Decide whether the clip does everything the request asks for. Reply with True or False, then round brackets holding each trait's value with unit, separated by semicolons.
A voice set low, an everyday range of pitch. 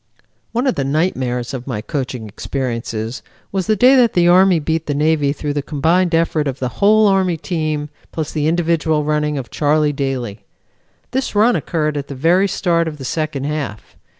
False (150 Hz; 4.0 semitones)